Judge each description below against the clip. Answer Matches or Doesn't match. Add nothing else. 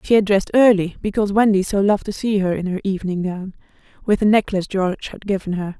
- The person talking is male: Doesn't match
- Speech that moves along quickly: Matches